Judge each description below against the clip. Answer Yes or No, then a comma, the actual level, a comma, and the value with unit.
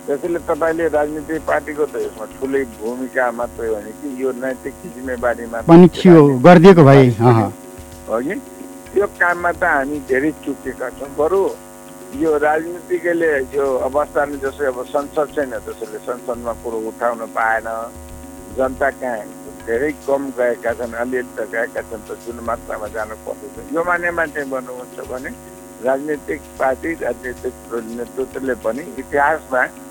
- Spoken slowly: Yes, slow, 110 wpm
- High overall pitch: No, low, 130 Hz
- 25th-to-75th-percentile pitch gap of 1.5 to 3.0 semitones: No, average, 4.2 semitones